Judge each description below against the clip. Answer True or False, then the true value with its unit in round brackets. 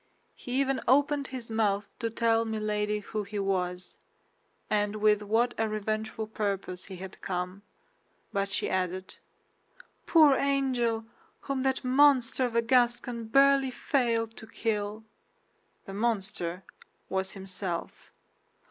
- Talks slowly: True (125 wpm)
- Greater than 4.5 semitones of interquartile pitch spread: False (3.7 semitones)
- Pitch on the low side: False (220 Hz)